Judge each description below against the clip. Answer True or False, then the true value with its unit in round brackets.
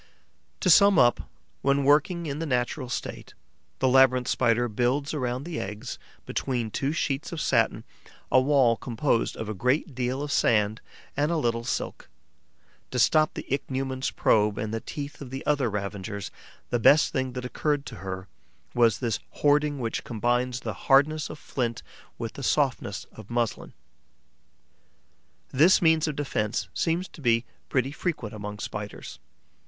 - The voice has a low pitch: True (130 Hz)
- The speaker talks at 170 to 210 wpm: False (160 wpm)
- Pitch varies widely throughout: False (4.0 semitones)